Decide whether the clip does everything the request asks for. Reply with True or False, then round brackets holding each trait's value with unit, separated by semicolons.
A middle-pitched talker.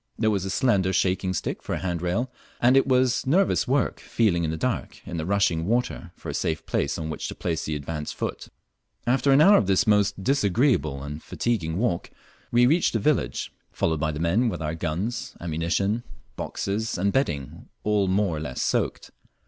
False (100 Hz)